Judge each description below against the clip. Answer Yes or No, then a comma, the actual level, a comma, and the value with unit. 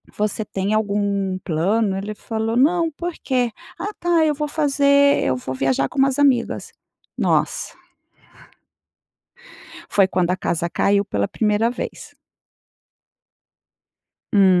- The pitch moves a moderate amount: No, wide, 6.6 semitones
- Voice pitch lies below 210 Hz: No, high, 215 Hz